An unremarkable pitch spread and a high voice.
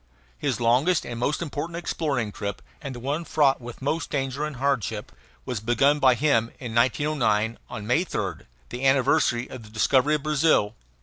No: average, 4.1 semitones; low, 130 Hz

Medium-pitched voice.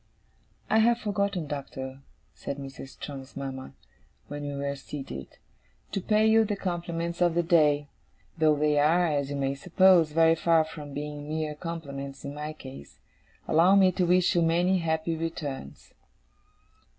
Yes: medium, 155 Hz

